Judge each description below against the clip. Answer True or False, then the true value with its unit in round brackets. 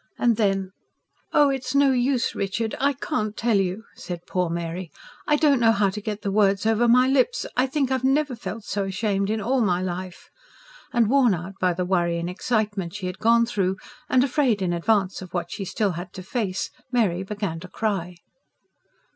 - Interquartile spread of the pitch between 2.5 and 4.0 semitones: False (4.6 semitones)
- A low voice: False (205 Hz)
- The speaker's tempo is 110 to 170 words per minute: False (195 wpm)